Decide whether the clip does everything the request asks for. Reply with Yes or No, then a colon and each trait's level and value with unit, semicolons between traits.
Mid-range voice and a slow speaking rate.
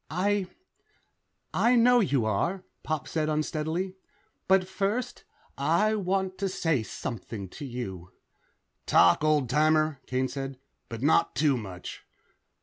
Yes: medium, 155 Hz; slow, 125 wpm